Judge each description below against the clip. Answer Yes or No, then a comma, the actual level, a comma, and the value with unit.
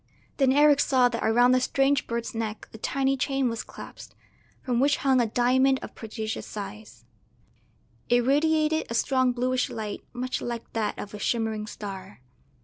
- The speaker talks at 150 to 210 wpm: Yes, average, 165 wpm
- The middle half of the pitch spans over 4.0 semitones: No, average, 3.3 semitones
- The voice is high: Yes, high, 245 Hz